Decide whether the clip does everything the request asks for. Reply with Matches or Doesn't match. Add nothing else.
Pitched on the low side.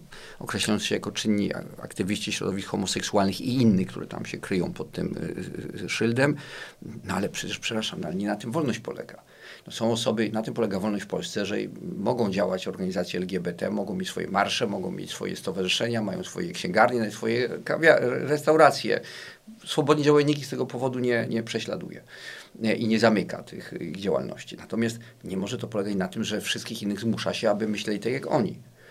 Matches